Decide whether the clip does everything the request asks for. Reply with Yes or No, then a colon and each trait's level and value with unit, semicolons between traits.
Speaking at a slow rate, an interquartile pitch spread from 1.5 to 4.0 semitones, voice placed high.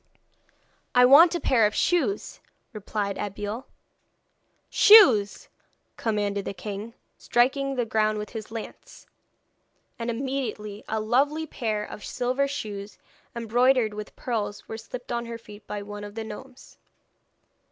Yes: slow, 130 wpm; average, 3.3 semitones; high, 225 Hz